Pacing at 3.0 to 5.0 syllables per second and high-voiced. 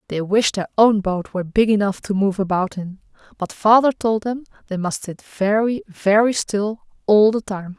Yes: 4.7 syllables/s; high, 205 Hz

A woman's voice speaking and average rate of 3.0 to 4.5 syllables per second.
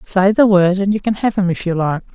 No: female; 5.6 syllables/s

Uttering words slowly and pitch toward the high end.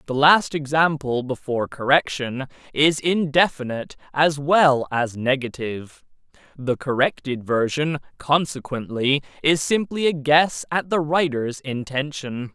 No: slow, 110 wpm; medium, 140 Hz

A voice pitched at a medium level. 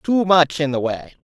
Yes: medium, 160 Hz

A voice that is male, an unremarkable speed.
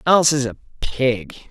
Yes: male; average, 160 wpm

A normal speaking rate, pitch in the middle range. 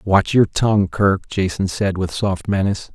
No: average, 185 wpm; very low, 95 Hz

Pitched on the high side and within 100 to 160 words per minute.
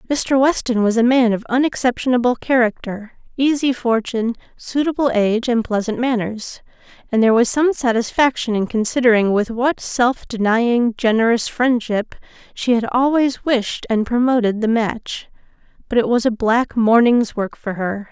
Yes: high, 235 Hz; average, 150 wpm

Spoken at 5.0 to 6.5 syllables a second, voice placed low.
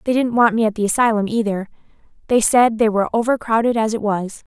No: 6.2 syllables/s; high, 220 Hz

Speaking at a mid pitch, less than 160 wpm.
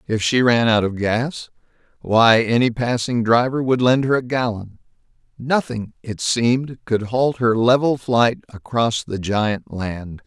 No: low, 120 Hz; average, 150 wpm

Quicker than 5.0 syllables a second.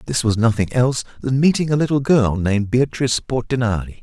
Yes: 6.0 syllables/s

